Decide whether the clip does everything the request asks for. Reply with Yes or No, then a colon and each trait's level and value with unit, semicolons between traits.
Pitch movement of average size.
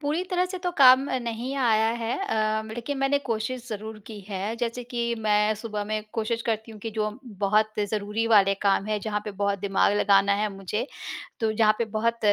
No: narrow, 2.2 semitones